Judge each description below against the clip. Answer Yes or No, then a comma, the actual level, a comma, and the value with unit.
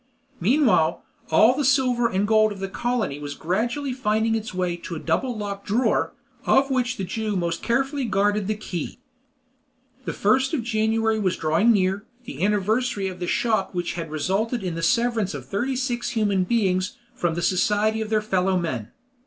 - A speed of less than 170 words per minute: No, average, 180 wpm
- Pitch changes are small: No, average, 4.3 semitones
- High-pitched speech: Yes, high, 210 Hz